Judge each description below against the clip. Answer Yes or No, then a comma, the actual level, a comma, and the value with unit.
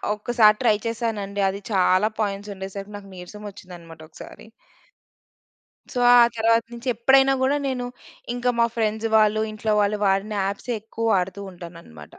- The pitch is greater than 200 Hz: Yes, high, 210 Hz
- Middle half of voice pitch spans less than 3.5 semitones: Yes, average, 3.0 semitones